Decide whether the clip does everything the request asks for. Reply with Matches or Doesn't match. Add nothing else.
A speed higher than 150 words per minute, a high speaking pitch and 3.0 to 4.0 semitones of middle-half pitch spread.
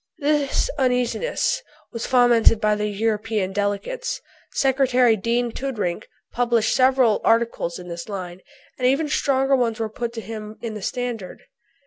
Doesn't match